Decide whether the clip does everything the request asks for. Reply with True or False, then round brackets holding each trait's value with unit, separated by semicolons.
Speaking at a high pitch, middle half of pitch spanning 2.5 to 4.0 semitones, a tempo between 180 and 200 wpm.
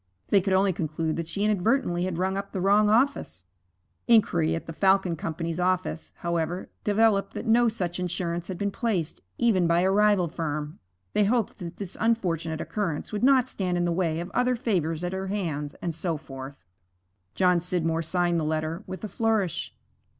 False (180 Hz; 3.6 semitones; 185 wpm)